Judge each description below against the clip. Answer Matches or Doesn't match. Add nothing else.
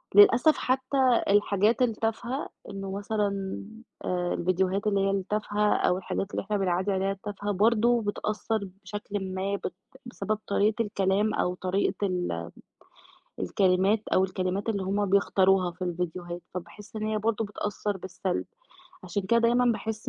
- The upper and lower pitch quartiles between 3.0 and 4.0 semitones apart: Doesn't match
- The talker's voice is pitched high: Matches